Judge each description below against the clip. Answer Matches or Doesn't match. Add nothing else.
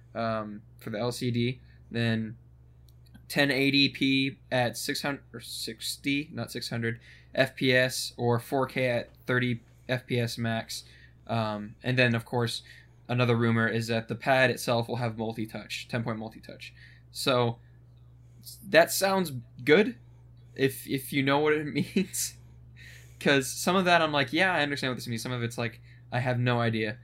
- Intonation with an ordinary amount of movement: Doesn't match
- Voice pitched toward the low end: Matches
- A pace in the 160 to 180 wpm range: Matches